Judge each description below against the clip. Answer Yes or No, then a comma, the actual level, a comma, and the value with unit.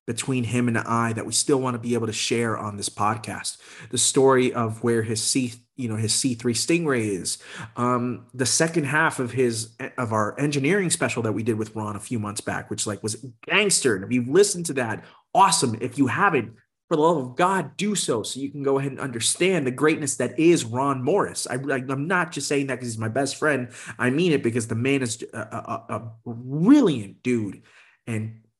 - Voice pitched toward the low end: Yes, low, 125 Hz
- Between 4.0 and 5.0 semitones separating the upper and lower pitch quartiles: No, average, 3.6 semitones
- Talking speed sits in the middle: No, fast, 225 wpm